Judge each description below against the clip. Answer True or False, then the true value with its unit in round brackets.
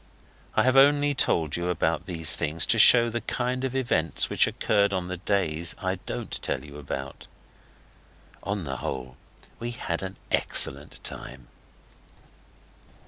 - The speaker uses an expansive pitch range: True (7.4 semitones)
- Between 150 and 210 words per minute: False (140 wpm)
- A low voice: True (90 Hz)